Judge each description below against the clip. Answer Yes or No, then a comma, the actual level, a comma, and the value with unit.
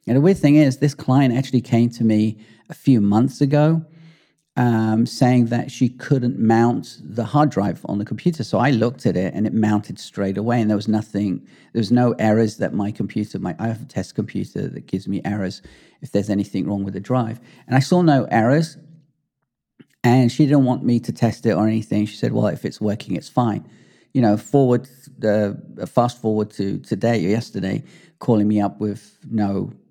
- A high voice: No, low, 115 Hz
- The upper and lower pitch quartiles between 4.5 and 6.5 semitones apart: No, average, 3.8 semitones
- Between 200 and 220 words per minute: Yes, fast, 205 wpm